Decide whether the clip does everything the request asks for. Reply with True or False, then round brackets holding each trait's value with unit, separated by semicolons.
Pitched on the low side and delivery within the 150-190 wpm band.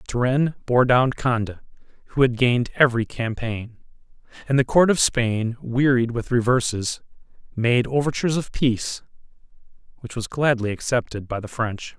False (120 Hz; 140 wpm)